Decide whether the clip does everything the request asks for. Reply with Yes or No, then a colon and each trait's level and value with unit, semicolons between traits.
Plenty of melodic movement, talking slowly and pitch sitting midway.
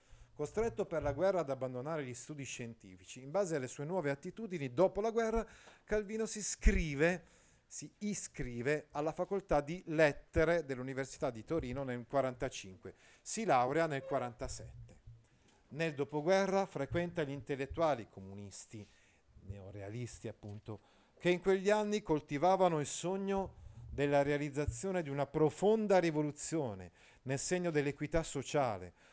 No: wide, 6.2 semitones; average, 125 wpm; medium, 145 Hz